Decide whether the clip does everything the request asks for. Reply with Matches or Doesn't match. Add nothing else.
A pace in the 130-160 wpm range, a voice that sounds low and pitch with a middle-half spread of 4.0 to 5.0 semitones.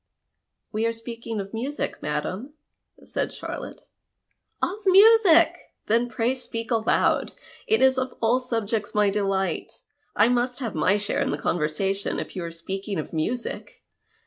Doesn't match